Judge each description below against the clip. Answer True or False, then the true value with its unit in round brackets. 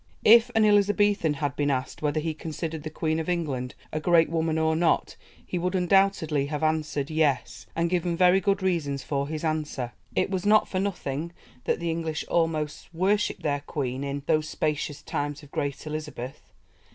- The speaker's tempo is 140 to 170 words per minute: False (180 wpm)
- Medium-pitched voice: True (160 Hz)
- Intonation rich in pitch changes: False (3.2 semitones)